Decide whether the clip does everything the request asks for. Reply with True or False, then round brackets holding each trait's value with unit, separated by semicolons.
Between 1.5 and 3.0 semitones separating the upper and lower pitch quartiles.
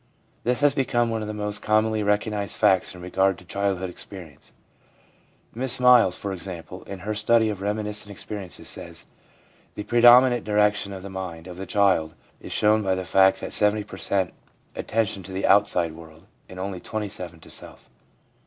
True (2.5 semitones)